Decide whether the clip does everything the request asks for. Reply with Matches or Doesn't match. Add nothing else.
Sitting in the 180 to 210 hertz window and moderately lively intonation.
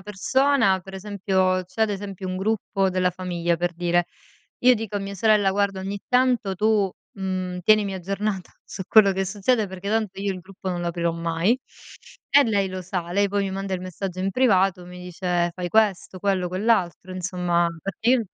Doesn't match